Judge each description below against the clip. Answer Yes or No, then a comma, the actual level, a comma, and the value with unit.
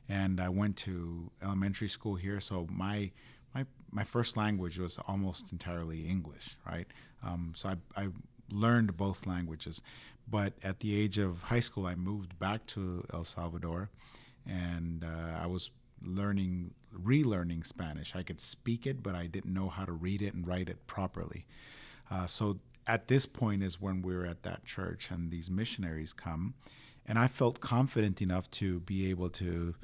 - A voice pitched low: Yes, very low, 95 Hz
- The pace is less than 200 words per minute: Yes, average, 175 wpm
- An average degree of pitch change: Yes, average, 3.2 semitones